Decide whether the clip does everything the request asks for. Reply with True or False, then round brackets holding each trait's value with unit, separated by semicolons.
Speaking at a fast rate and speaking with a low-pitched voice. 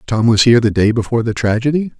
True (240 wpm; 115 Hz)